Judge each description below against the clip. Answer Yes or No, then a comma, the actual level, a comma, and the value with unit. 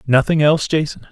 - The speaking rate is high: No, average, 160 wpm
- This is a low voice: No, medium, 150 Hz